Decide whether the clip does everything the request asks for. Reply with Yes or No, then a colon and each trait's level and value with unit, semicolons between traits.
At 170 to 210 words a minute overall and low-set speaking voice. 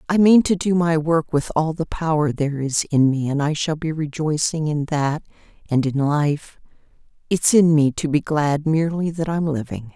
No: average, 200 wpm; medium, 155 Hz